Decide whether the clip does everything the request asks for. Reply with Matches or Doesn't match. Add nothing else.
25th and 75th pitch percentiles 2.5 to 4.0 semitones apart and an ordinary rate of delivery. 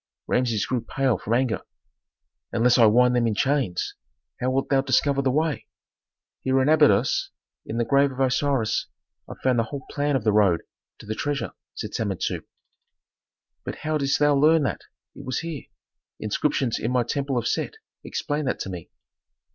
Matches